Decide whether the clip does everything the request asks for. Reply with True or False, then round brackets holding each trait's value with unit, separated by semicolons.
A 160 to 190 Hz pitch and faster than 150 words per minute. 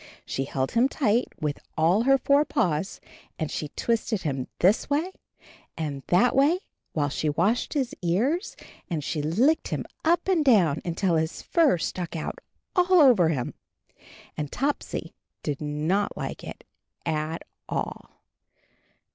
False (185 Hz; 145 wpm)